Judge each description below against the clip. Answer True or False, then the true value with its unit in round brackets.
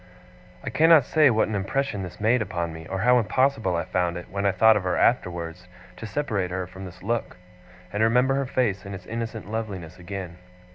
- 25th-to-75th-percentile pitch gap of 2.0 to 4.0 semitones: False (4.4 semitones)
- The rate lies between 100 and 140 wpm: False (205 wpm)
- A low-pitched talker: True (100 Hz)